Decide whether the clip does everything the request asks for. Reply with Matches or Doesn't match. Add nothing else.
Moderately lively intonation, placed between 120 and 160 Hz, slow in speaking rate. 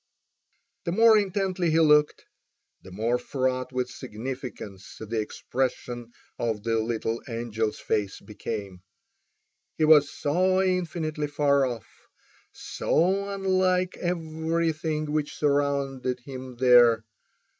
Doesn't match